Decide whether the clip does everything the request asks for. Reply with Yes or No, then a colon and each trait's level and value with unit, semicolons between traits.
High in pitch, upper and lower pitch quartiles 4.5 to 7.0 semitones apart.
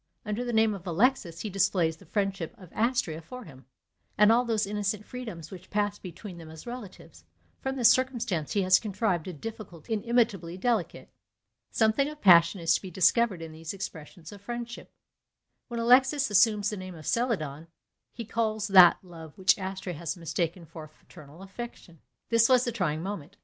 Yes: high, 195 Hz; average, 5.3 semitones